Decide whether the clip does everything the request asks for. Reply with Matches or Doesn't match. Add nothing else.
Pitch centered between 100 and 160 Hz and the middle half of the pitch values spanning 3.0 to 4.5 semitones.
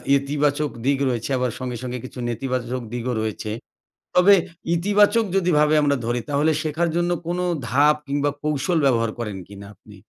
Matches